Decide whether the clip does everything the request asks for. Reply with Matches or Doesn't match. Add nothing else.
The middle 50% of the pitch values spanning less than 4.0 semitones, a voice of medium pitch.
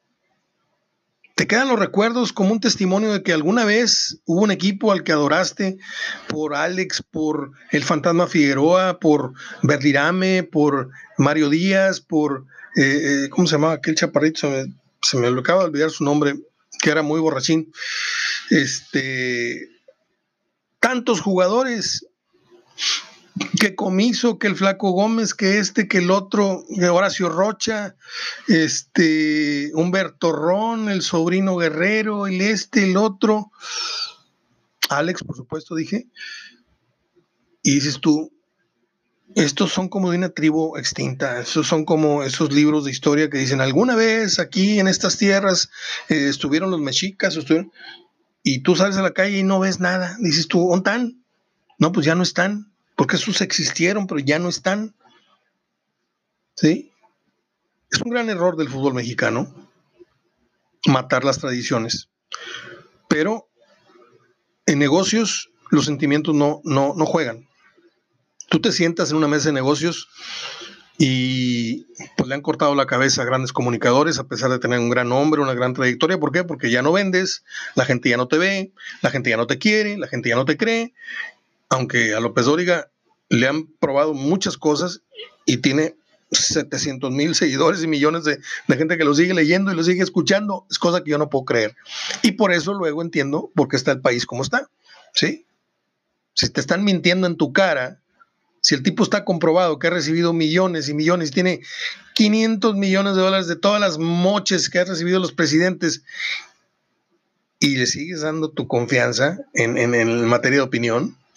Doesn't match